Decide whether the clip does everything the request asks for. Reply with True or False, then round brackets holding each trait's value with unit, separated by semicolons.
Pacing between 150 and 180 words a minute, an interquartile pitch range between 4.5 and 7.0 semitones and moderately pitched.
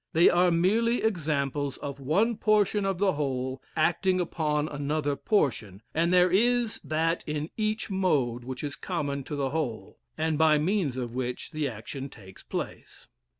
True (160 wpm; 5.1 semitones; 155 Hz)